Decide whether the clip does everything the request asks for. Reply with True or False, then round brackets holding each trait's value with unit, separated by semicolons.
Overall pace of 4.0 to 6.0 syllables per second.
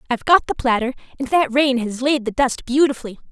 False (6.3 syllables/s)